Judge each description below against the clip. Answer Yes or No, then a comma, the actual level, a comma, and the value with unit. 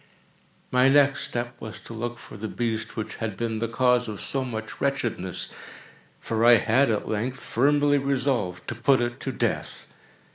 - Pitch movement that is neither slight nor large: Yes, average, 3.1 semitones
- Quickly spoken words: No, average, 175 wpm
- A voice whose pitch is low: Yes, low, 120 Hz